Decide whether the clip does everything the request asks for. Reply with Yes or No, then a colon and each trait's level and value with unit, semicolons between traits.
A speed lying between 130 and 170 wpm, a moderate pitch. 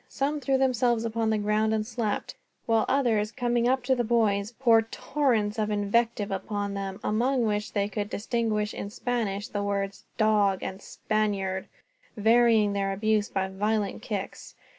No: average, 160 wpm; high, 215 Hz